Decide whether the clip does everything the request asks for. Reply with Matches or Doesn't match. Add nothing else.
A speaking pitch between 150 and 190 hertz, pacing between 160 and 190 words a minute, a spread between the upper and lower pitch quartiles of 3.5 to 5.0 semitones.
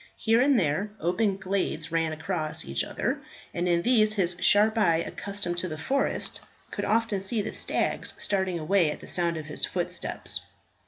Matches